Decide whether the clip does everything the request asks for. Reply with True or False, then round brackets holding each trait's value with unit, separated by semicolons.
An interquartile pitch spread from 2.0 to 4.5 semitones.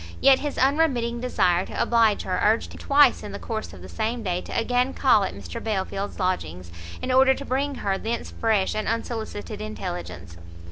False (5.1 semitones)